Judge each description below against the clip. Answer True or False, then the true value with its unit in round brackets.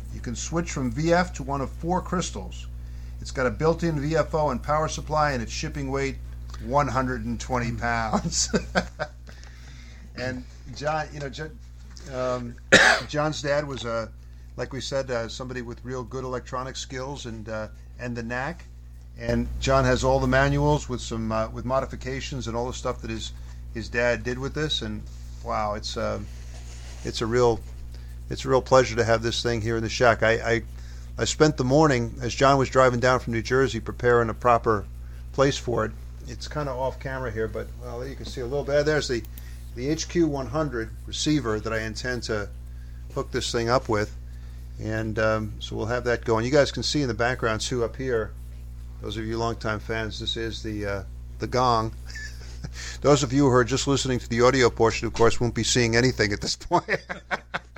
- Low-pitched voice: True (120 Hz)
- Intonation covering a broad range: False (4.9 semitones)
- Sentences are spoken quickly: False (195 wpm)